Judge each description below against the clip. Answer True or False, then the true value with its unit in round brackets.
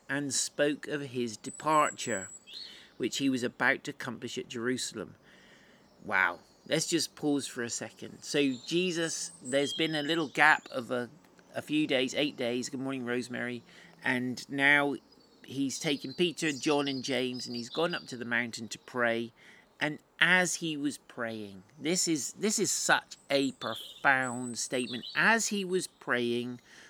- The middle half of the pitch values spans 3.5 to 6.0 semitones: True (3.8 semitones)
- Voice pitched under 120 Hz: False (135 Hz)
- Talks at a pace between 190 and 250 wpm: False (160 wpm)